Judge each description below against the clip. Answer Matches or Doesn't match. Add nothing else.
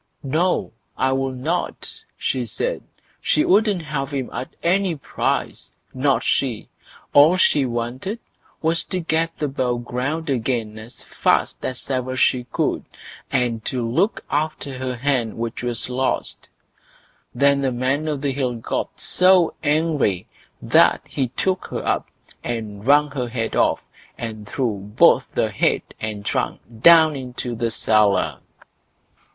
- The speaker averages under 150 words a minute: Matches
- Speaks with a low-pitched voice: Matches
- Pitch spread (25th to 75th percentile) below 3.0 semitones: Doesn't match